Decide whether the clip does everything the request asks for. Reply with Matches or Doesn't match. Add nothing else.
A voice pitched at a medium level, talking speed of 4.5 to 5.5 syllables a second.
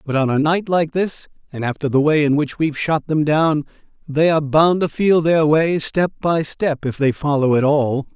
Matches